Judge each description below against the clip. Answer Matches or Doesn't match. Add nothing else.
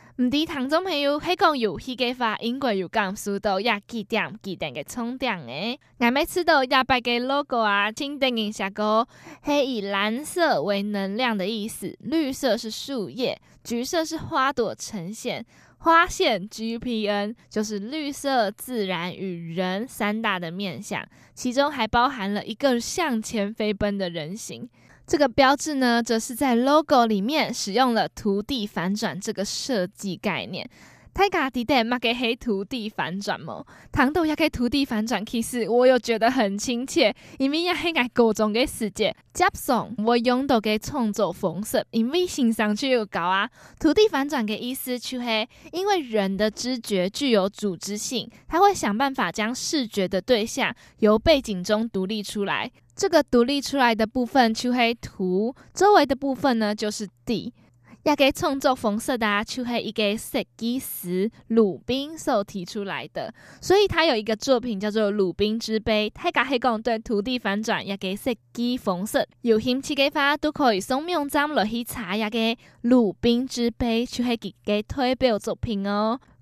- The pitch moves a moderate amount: Matches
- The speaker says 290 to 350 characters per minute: Doesn't match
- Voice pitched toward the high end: Matches